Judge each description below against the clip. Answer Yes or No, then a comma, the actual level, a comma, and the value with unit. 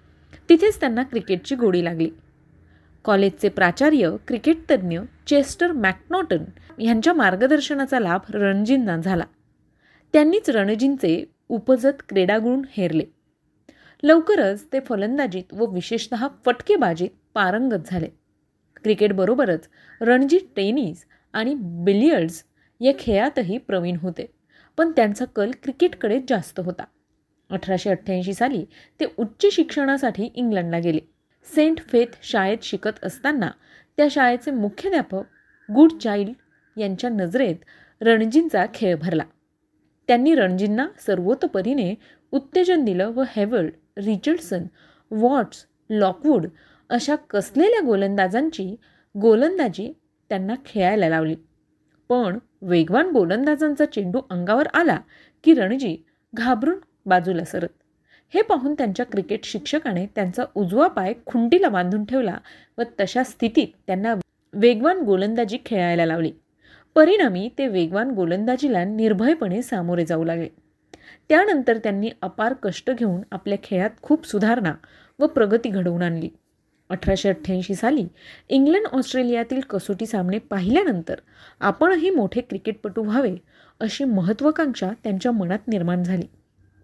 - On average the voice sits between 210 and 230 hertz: Yes, high, 225 Hz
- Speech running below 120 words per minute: Yes, average, 105 wpm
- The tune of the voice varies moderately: No, wide, 6.2 semitones